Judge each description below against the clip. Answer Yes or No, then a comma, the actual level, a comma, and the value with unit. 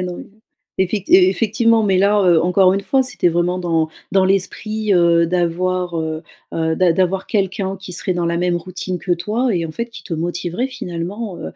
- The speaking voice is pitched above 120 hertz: Yes, medium, 185 Hz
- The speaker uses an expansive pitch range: No, narrow, 2.4 semitones